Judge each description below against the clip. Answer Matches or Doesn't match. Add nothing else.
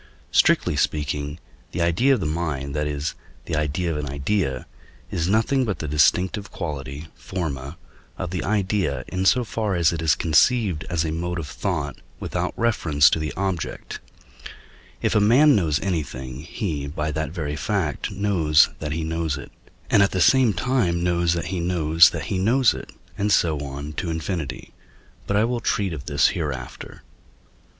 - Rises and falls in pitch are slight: Doesn't match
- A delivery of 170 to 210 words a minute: Matches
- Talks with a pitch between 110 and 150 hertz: Doesn't match